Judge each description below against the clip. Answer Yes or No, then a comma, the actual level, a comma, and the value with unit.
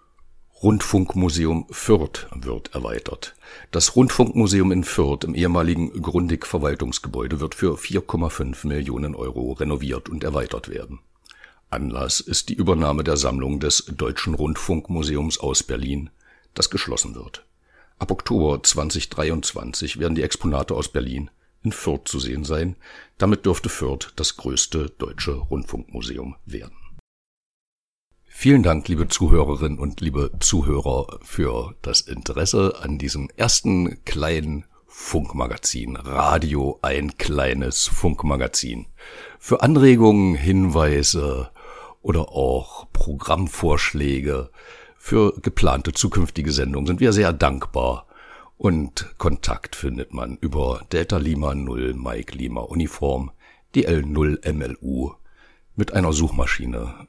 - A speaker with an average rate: No, slow, 110 wpm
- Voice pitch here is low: Yes, very low, 75 Hz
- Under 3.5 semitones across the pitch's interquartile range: No, average, 4.0 semitones